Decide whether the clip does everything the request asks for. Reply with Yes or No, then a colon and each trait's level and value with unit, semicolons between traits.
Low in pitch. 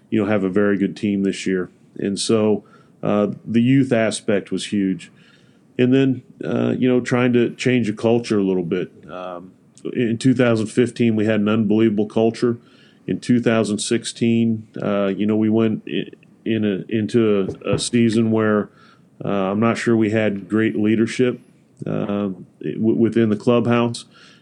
Yes: low, 110 Hz